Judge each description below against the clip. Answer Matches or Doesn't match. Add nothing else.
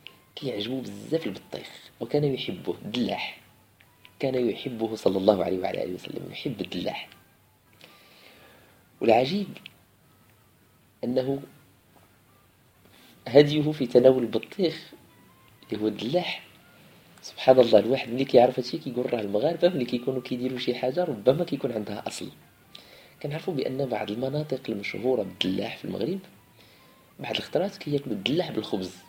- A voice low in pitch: Matches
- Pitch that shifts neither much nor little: Matches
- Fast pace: Doesn't match